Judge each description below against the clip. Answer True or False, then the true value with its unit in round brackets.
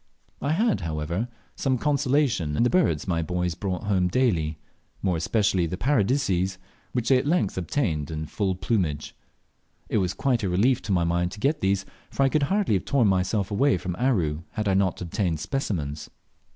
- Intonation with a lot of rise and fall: True (6.7 semitones)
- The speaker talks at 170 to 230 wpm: True (185 wpm)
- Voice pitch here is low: True (95 Hz)